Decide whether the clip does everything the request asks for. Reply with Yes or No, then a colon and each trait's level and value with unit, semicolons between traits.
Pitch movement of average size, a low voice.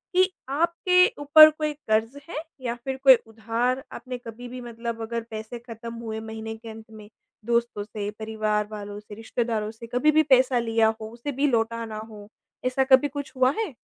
No: average, 3.0 semitones; high, 235 Hz